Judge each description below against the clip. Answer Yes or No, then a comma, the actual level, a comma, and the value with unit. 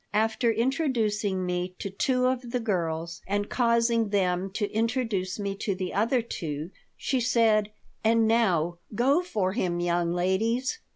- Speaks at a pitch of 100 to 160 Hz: No, high, 210 Hz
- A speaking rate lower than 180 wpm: Yes, average, 150 wpm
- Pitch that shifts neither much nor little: Yes, average, 4.3 semitones